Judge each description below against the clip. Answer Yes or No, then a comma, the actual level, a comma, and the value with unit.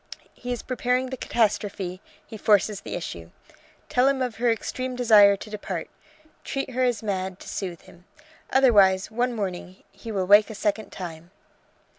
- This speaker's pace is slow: No, average, 165 wpm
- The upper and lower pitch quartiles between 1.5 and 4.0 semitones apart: No, average, 4.5 semitones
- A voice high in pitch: Yes, high, 210 Hz